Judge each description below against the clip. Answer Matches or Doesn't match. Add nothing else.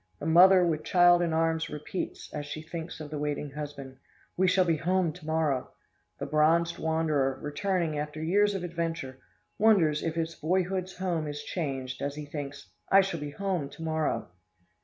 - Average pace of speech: Matches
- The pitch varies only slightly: Doesn't match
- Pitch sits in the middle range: Matches